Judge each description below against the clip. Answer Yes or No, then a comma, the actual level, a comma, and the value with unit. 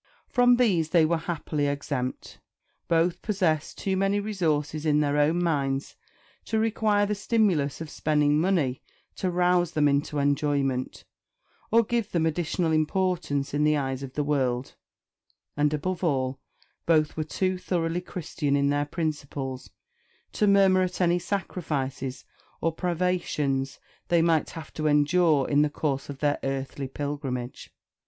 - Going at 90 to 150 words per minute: Yes, average, 145 wpm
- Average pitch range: Yes, average, 4.0 semitones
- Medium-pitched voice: Yes, medium, 155 Hz